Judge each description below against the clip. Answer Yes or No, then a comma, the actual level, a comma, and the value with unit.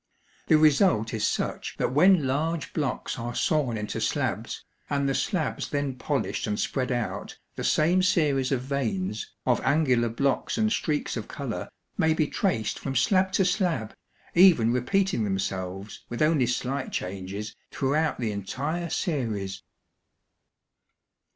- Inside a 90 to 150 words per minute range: Yes, average, 140 wpm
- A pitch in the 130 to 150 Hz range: Yes, low, 135 Hz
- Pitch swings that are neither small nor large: No, wide, 5.9 semitones